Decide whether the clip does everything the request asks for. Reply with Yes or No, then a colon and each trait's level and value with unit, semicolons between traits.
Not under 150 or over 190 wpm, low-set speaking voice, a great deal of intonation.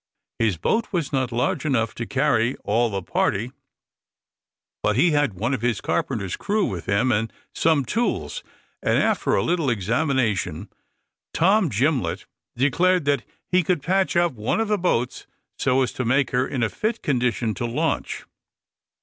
Yes: average, 165 wpm; low, 130 Hz; wide, 6.1 semitones